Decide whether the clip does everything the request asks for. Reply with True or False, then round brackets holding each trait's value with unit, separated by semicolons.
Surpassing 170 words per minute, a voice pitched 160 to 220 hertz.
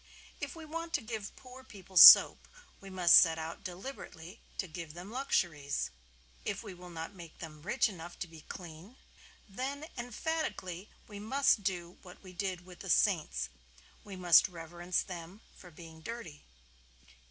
False (160 wpm; 185 Hz)